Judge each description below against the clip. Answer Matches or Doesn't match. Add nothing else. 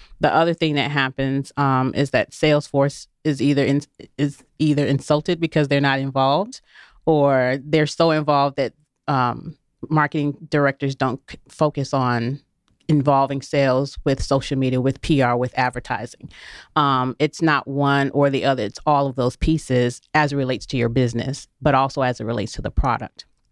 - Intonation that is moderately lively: Doesn't match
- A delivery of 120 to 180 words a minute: Matches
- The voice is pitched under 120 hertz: Doesn't match